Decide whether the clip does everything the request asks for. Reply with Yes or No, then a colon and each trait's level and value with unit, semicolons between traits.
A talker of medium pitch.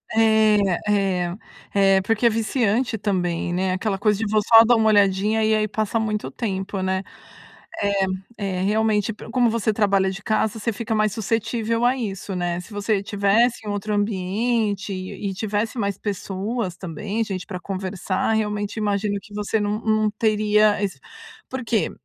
No: high, 210 Hz